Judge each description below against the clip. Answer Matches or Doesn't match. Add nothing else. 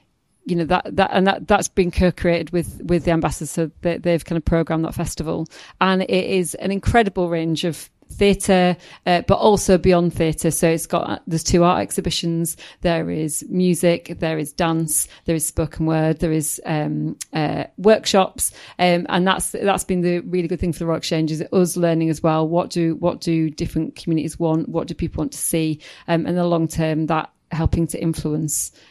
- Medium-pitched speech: Matches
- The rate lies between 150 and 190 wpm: Doesn't match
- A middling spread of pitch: Doesn't match